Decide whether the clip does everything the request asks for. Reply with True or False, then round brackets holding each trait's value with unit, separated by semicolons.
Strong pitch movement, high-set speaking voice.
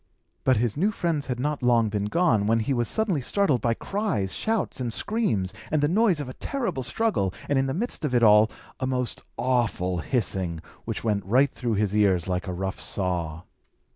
False (6.6 semitones; 120 Hz)